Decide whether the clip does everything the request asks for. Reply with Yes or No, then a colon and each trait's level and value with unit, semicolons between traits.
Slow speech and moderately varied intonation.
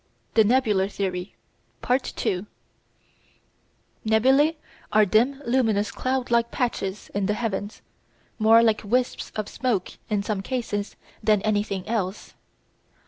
Yes: slow, 120 wpm; average, 3.2 semitones